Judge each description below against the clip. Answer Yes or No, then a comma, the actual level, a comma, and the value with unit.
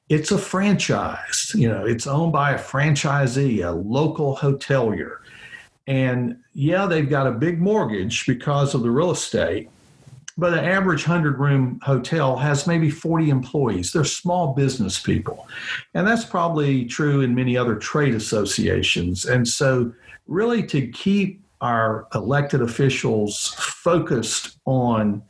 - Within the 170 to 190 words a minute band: No, average, 140 wpm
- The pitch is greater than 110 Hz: Yes, medium, 140 Hz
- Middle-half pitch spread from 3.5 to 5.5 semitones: Yes, average, 5.0 semitones